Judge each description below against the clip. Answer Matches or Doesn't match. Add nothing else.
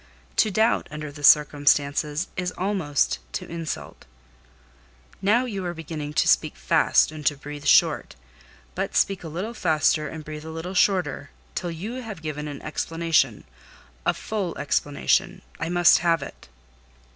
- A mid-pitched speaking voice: Matches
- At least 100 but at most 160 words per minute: Matches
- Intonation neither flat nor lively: Matches